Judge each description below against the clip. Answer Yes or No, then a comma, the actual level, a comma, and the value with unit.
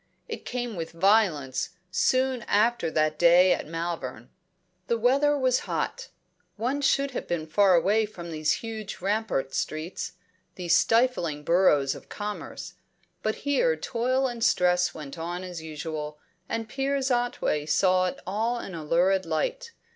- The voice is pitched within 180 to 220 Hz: Yes, high, 190 Hz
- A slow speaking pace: No, average, 145 wpm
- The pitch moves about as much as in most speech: No, wide, 6.6 semitones